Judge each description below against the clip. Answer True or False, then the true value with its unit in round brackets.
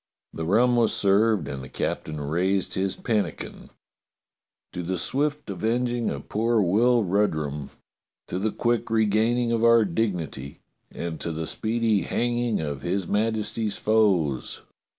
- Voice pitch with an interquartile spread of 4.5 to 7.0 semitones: True (5.1 semitones)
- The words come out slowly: False (145 wpm)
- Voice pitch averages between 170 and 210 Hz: False (105 Hz)